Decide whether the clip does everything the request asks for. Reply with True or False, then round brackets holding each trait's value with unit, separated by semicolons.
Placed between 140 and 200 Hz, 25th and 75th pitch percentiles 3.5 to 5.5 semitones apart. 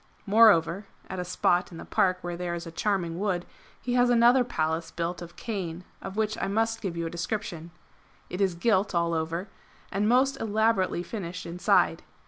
True (185 Hz; 4.2 semitones)